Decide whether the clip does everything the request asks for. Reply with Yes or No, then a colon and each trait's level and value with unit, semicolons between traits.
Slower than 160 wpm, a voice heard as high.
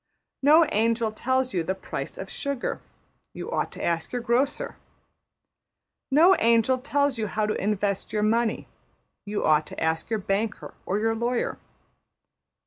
Yes: average, 150 wpm; high, 225 Hz